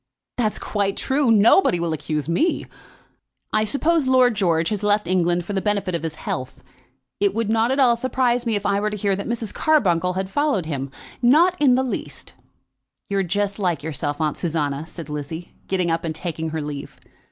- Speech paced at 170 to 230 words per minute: Yes, average, 195 wpm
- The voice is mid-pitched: No, high, 200 Hz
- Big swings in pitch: Yes, wide, 6.1 semitones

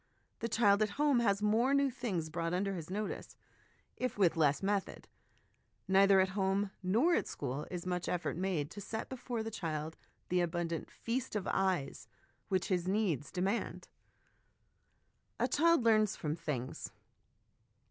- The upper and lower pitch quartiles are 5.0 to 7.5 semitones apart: No, average, 4.4 semitones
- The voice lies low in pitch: No, high, 195 Hz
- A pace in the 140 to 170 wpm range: Yes, average, 155 wpm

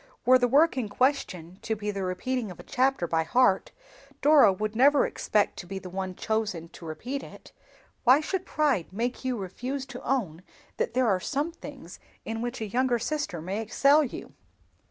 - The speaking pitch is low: No, high, 235 Hz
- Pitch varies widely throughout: Yes, wide, 5.9 semitones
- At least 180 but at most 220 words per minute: Yes, average, 190 wpm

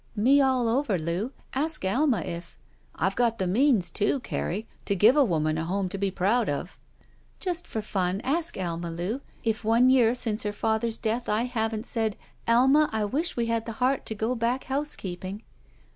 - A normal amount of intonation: Yes, average, 4.4 semitones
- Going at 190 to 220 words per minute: Yes, average, 195 wpm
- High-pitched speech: Yes, high, 225 Hz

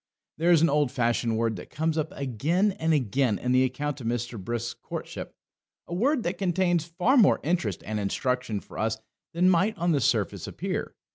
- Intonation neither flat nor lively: No, wide, 6.5 semitones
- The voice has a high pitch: No, medium, 145 Hz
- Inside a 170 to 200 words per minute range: Yes, average, 195 wpm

